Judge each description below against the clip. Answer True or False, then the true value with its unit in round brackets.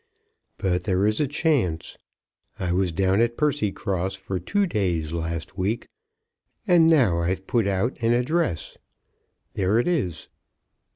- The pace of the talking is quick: False (135 wpm)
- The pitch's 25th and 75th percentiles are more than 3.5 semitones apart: True (5.4 semitones)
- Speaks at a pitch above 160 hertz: False (100 Hz)